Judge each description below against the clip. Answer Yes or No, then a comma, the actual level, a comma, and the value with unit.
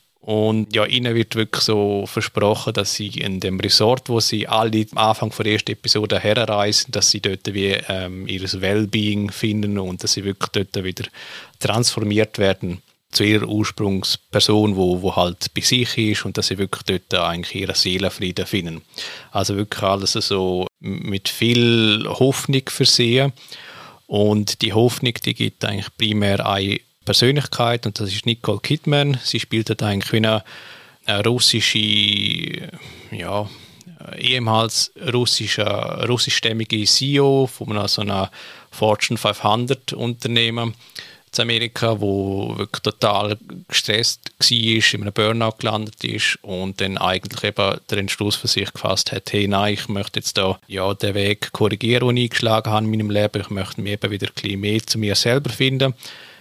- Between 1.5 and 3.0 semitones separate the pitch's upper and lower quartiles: Yes, average, 2.7 semitones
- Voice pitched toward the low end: Yes, low, 105 Hz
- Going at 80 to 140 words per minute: No, average, 155 wpm